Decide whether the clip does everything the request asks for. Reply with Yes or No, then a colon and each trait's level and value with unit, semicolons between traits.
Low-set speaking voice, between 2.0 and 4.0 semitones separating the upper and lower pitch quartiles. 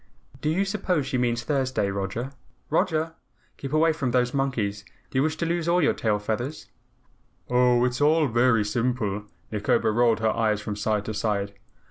No: low, 125 Hz; wide, 5.6 semitones